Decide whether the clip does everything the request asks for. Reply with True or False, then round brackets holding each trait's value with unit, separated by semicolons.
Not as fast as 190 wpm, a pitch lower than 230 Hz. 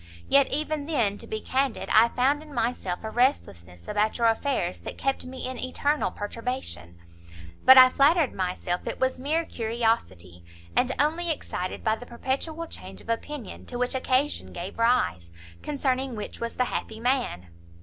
False (165 wpm; 250 Hz)